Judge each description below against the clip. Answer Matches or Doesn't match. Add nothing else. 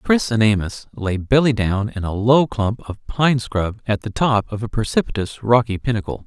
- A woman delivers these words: Doesn't match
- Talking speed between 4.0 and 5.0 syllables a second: Matches